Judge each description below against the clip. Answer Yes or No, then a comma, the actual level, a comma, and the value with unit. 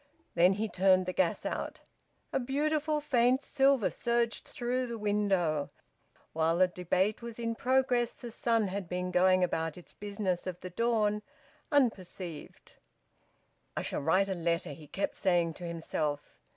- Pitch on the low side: No, high, 195 Hz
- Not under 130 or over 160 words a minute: Yes, average, 150 wpm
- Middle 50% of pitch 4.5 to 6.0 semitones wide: Yes, average, 5.0 semitones